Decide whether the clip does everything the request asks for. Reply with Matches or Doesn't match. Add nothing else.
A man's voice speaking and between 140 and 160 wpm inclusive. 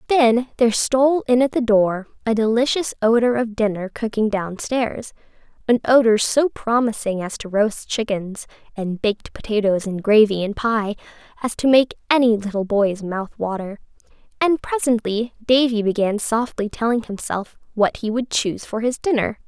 Doesn't match